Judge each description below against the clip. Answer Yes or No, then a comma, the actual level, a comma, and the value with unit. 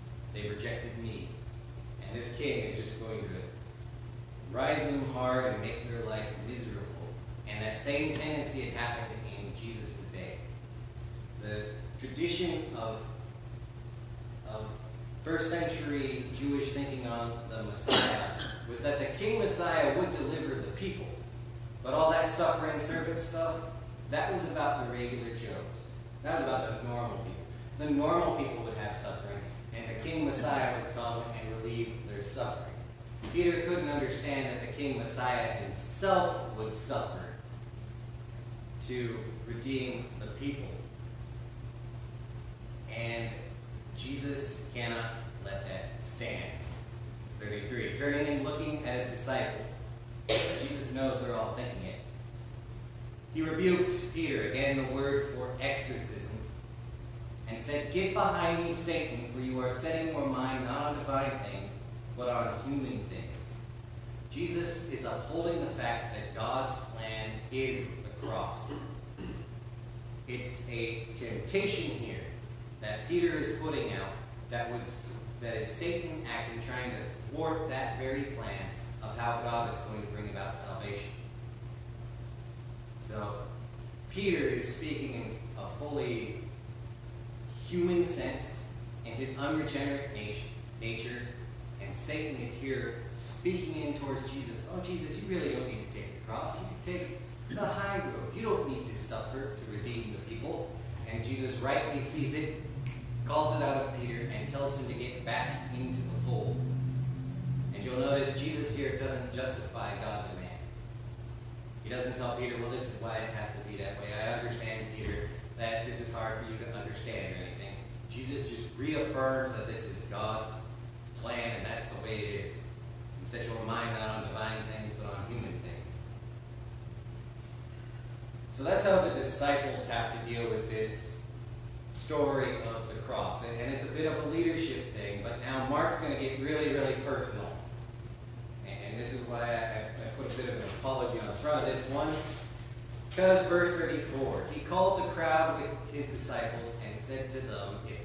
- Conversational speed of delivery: Yes, average, 155 wpm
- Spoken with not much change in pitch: Yes, narrow, 2.2 semitones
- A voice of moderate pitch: No, low, 120 Hz